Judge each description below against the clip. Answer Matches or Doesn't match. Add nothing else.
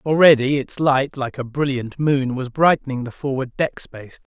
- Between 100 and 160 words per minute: Doesn't match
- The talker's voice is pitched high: Doesn't match